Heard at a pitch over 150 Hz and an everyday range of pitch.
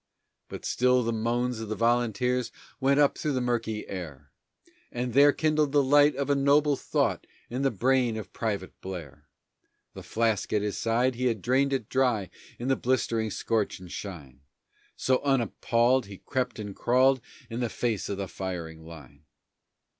No: low, 120 Hz; average, 4.1 semitones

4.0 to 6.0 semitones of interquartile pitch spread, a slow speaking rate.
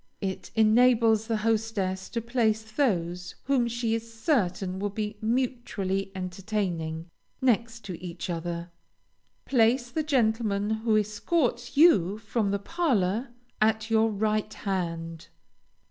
No: average, 3.5 semitones; slow, 115 wpm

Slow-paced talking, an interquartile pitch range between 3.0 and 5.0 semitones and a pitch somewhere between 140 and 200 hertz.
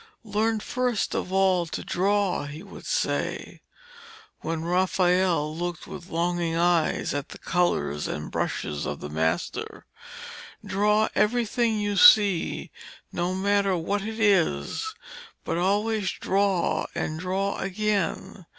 Yes: slow, 125 wpm; average, 3.3 semitones; high, 190 Hz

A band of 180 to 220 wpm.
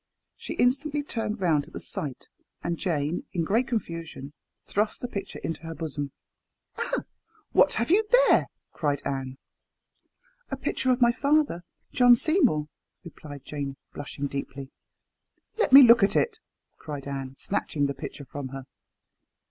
No: average, 155 wpm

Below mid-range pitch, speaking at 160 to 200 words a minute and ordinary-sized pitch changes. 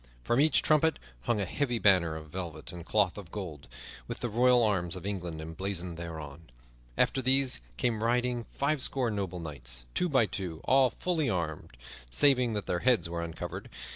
No: low, 100 Hz; average, 170 wpm; wide, 6.8 semitones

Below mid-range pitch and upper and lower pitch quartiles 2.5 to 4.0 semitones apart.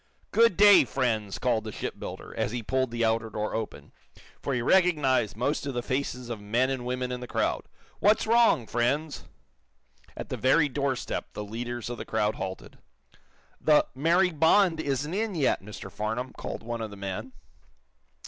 No: low, 125 Hz; average, 4.9 semitones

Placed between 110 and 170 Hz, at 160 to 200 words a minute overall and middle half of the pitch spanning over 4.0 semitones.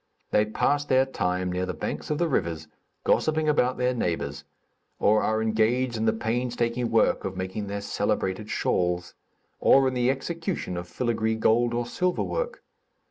Yes: low, 115 Hz; average, 165 wpm; average, 4.7 semitones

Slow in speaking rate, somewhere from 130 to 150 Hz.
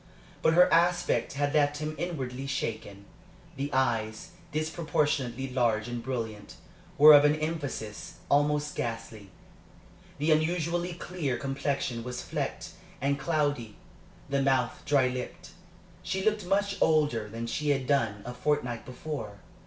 Yes: slow, 130 wpm; medium, 140 Hz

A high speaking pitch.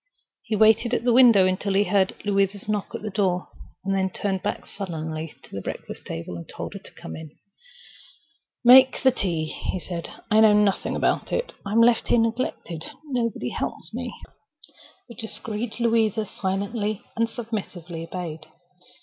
Yes: high, 205 Hz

